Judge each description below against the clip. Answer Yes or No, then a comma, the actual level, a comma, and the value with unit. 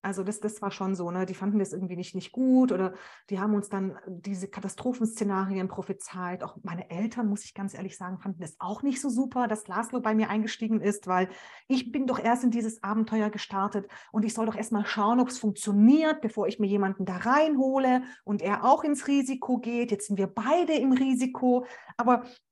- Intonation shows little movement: No, average, 4.2 semitones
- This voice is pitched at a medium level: No, high, 210 Hz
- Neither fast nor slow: No, fast, 210 wpm